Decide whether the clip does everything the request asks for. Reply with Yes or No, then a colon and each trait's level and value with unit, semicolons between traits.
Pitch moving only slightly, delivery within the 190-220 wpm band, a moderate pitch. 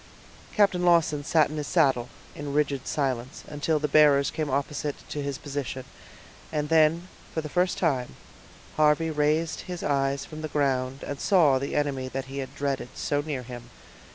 No: narrow, 2.2 semitones; average, 170 wpm; medium, 145 Hz